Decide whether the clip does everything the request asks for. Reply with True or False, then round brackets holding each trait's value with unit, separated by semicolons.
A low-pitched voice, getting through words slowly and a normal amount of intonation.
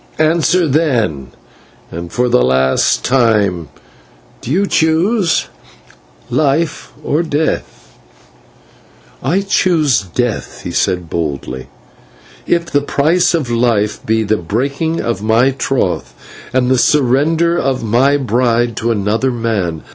False (125 Hz; 115 wpm; 6.7 semitones)